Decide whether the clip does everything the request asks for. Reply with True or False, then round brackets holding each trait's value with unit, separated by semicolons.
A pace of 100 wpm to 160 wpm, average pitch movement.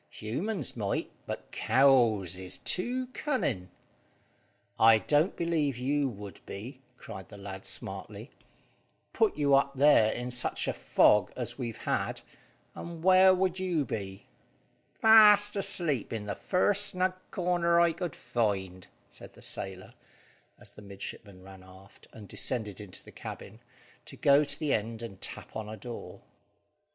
False (145 wpm; 8.9 semitones)